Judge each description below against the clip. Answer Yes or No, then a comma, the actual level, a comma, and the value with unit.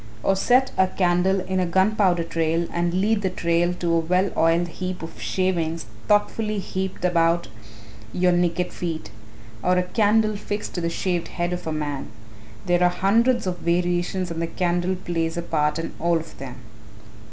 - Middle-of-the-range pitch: Yes, medium, 175 Hz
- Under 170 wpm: No, average, 175 wpm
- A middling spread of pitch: No, narrow, 2.0 semitones